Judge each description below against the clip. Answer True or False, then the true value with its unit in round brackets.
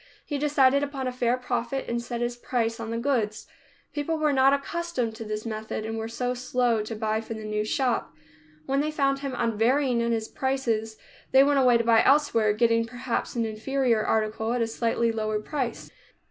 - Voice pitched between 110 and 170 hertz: False (240 Hz)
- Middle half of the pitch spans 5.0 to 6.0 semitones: False (3.3 semitones)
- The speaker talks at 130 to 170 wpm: False (200 wpm)